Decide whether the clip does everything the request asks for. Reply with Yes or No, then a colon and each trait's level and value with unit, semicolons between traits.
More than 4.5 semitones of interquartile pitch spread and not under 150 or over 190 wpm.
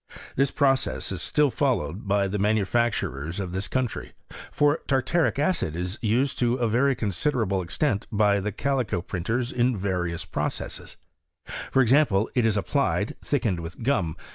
Yes: wide, 5.6 semitones; average, 155 wpm